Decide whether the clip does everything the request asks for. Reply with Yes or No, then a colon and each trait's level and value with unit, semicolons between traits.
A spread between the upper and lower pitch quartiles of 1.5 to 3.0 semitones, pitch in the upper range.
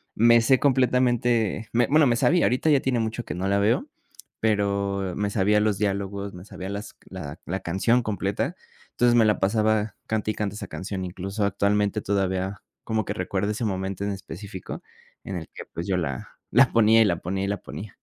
No: average, 2.7 semitones; low, 100 Hz